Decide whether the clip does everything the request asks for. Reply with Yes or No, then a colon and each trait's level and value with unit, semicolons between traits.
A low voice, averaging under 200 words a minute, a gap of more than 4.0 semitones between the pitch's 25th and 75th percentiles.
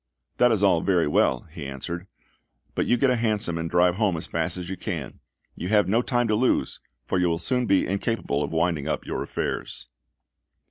No: very low, 90 Hz; fast, 205 wpm; average, 4.7 semitones